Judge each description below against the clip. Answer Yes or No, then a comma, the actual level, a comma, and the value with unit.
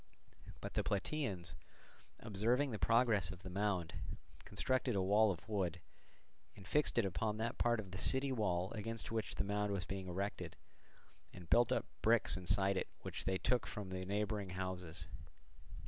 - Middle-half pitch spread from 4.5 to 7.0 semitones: No, average, 3.4 semitones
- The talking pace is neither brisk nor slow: Yes, average, 165 wpm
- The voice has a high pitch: No, low, 100 Hz